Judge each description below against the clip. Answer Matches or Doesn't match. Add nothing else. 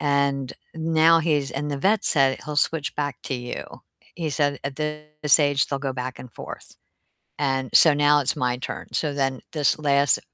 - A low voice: Doesn't match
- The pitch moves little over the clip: Matches